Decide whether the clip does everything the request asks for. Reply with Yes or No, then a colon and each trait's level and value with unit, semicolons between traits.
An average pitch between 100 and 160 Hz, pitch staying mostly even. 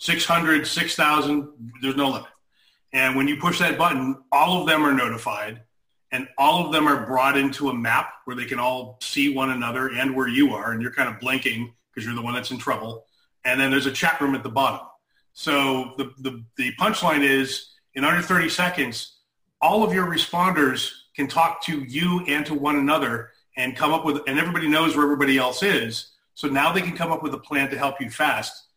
No: medium, 140 Hz; average, 3.4 semitones